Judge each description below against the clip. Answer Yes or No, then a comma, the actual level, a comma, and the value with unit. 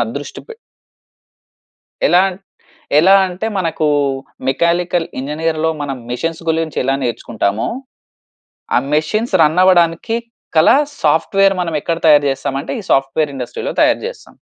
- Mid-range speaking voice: Yes, medium, 160 Hz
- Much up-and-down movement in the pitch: No, average, 3.6 semitones